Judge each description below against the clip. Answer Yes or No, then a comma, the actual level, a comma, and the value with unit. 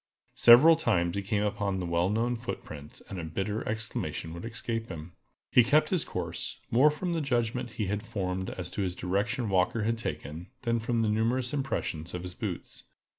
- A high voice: No, low, 105 Hz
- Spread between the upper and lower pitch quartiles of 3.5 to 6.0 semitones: Yes, average, 4.6 semitones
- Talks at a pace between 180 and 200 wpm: Yes, average, 190 wpm